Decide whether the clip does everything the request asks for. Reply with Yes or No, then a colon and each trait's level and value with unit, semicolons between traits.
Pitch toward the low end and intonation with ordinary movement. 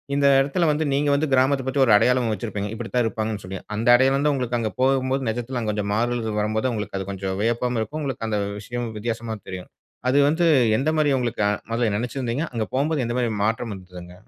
Yes: low, 120 Hz; average, 3.6 semitones